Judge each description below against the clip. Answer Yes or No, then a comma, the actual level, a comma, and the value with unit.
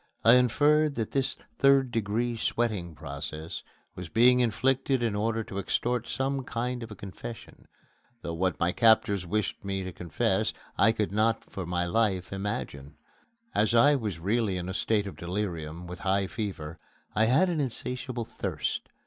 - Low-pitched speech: Yes, low, 110 Hz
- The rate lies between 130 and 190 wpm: Yes, average, 165 wpm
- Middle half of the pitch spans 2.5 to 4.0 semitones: No, average, 4.7 semitones